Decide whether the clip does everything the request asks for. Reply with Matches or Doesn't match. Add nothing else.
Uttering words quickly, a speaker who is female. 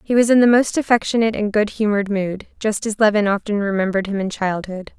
Matches